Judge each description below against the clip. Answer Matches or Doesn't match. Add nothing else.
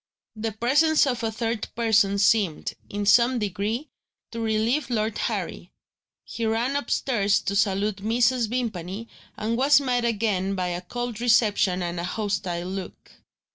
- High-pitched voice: Matches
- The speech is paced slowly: Doesn't match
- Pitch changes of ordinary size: Matches